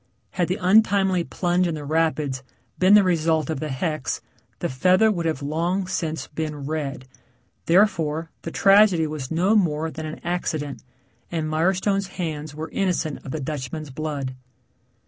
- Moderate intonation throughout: Yes, average, 3.3 semitones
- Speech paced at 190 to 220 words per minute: No, average, 155 wpm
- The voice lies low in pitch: No, medium, 160 Hz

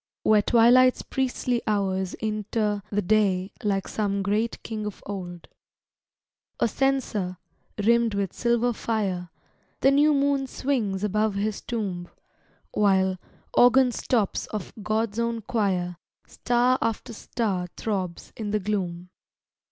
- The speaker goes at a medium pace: No, slow, 120 wpm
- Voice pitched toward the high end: Yes, high, 210 Hz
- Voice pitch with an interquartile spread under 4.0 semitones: Yes, average, 3.3 semitones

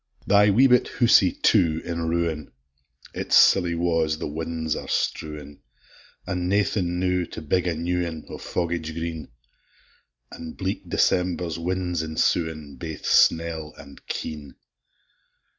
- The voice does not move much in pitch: Yes, narrow, 2.1 semitones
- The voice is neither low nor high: No, very low, 85 Hz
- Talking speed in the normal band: No, slow, 130 wpm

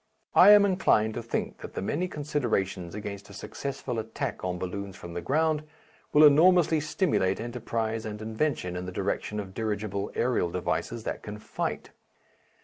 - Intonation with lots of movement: Yes, wide, 6.7 semitones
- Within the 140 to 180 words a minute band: Yes, average, 160 wpm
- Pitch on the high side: No, low, 110 Hz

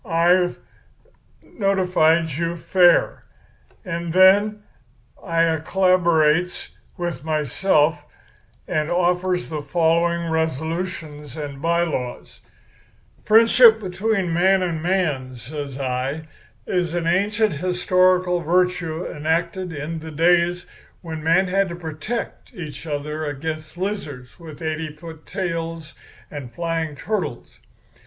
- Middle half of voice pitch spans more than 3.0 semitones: No, average, 2.7 semitones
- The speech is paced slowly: Yes, slow, 105 wpm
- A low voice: No, medium, 170 Hz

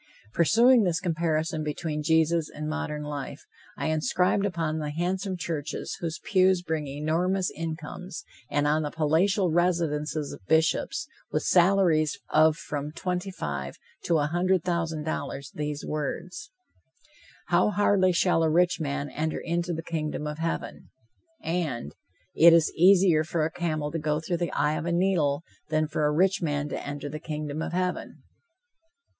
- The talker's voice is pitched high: No, medium, 160 Hz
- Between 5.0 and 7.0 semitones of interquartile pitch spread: No, average, 2.7 semitones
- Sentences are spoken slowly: No, average, 160 wpm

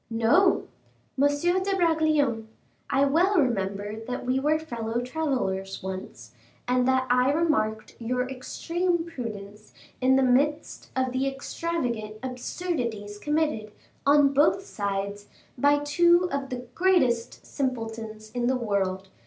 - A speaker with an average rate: No, slow, 130 wpm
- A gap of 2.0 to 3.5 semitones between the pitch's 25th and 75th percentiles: No, average, 5.2 semitones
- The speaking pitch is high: Yes, very high, 255 Hz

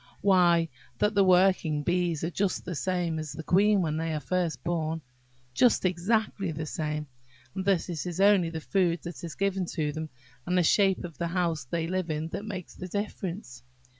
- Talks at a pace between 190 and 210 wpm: Yes, average, 195 wpm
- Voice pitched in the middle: Yes, medium, 175 Hz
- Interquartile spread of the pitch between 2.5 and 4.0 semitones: Yes, average, 3.0 semitones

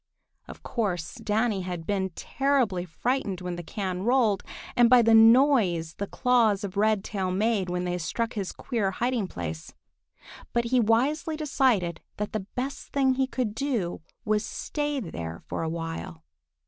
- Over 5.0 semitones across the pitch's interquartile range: Yes, wide, 5.5 semitones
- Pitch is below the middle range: No, high, 210 Hz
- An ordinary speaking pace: Yes, average, 160 wpm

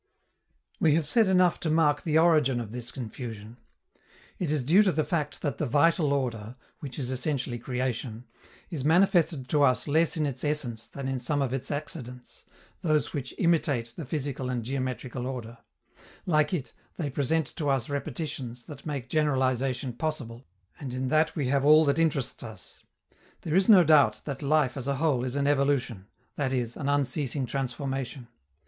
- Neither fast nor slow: Yes, average, 175 wpm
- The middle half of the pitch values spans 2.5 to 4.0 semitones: Yes, average, 3.5 semitones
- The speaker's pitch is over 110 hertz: Yes, medium, 140 Hz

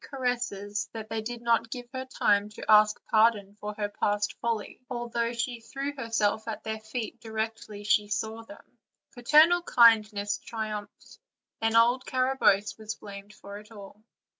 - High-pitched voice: Yes, high, 220 Hz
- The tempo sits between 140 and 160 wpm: Yes, average, 155 wpm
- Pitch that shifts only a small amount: Yes, narrow, 2.3 semitones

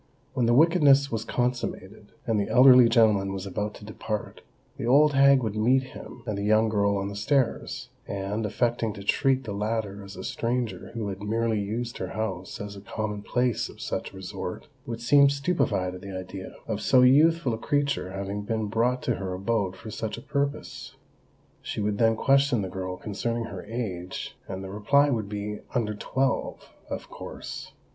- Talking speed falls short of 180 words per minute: No, average, 185 wpm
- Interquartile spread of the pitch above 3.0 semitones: Yes, average, 3.7 semitones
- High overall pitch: No, low, 110 Hz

